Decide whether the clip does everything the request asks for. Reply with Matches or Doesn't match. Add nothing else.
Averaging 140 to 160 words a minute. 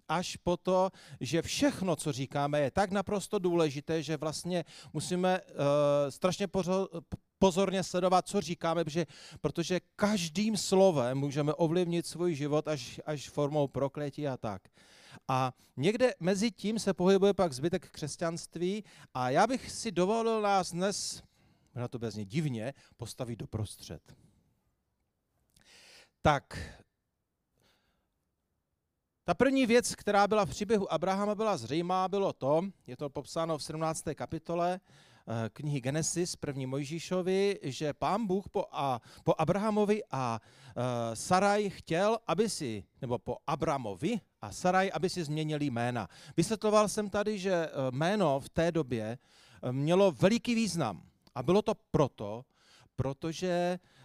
Doesn't match